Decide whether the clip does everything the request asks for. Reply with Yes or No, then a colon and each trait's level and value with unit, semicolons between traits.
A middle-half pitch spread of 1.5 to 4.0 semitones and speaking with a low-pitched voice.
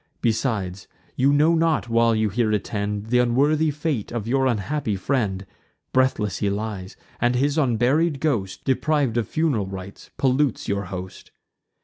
No: wide, 5.4 semitones; low, 120 Hz